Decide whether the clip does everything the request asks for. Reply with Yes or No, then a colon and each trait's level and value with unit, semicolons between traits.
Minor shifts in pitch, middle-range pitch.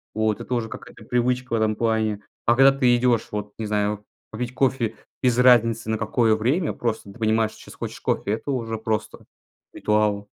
No: narrow, 2.3 semitones; low, 115 Hz